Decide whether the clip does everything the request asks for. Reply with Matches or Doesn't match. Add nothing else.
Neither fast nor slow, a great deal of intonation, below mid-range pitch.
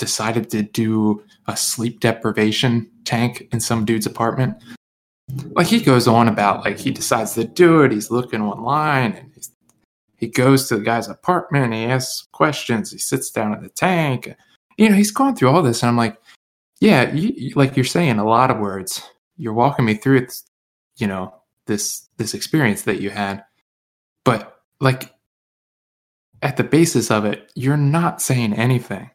Doesn't match